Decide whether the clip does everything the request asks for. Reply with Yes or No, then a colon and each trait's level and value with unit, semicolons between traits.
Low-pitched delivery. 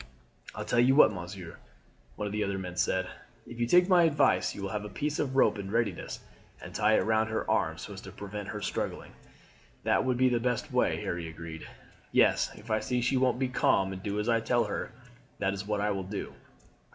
Yes: low, 105 Hz